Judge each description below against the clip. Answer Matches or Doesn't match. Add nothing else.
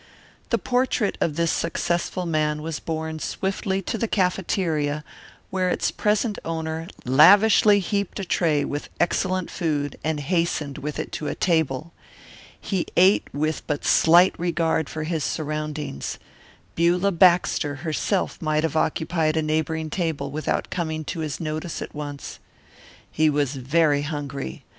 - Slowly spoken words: Doesn't match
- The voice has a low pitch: Doesn't match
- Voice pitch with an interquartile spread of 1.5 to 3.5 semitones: Matches